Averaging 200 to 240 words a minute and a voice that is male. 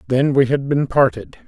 Yes: fast, 205 wpm; male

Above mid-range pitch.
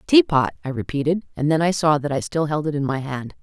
No: medium, 150 Hz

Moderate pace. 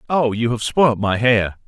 No: fast, 215 wpm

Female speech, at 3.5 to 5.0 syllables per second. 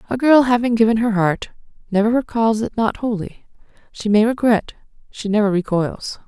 No: female; 5.2 syllables/s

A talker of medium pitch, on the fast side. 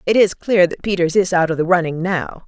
Yes: medium, 180 Hz; fast, 265 wpm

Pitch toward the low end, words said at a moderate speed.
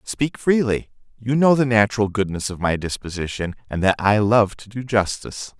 Yes: low, 110 Hz; average, 180 wpm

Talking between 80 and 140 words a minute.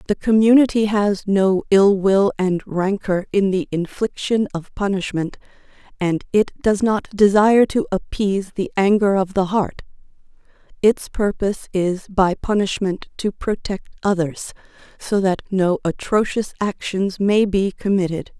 Yes: slow, 135 wpm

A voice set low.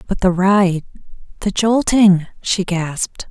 No: high, 190 Hz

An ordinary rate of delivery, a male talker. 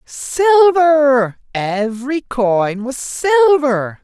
No: slow, 75 wpm; male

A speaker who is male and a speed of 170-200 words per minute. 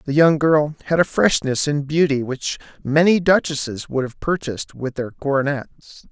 No: male; average, 155 wpm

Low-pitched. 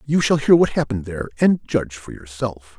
Yes: low, 120 Hz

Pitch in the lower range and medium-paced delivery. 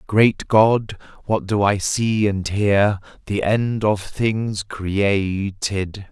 No: low, 100 Hz; slow, 130 wpm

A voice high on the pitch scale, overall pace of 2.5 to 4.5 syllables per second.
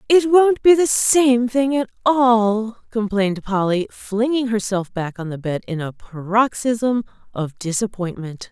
Yes: high, 225 Hz; 4.0 syllables/s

